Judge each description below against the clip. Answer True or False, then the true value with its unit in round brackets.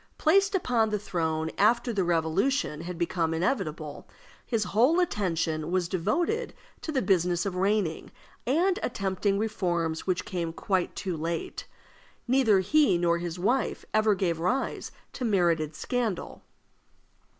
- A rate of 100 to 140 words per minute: True (135 wpm)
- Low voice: False (190 Hz)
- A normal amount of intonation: False (5.7 semitones)